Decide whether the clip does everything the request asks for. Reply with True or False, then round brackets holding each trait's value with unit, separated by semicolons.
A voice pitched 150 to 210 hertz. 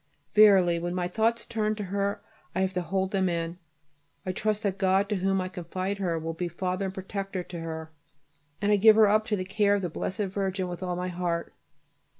True (190 Hz)